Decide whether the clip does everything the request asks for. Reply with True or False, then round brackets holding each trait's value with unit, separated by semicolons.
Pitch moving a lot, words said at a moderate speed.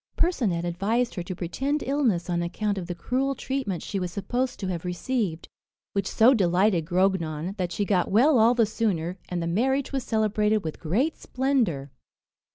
True (6.0 semitones; 175 wpm)